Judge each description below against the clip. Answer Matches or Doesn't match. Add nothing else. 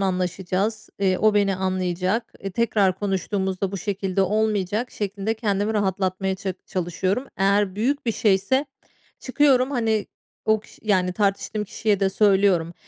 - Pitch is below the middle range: Doesn't match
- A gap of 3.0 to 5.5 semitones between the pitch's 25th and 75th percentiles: Doesn't match